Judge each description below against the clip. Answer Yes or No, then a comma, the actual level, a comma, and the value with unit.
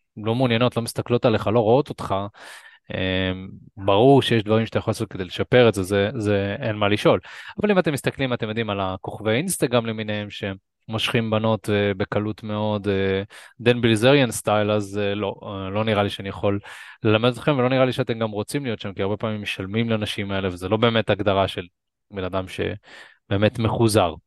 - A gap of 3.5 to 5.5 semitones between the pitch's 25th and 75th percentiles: No, narrow, 2.6 semitones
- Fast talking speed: Yes, fast, 180 wpm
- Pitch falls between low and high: No, low, 105 Hz